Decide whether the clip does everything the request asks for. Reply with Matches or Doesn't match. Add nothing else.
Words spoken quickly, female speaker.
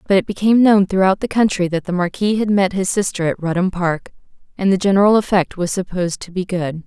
Matches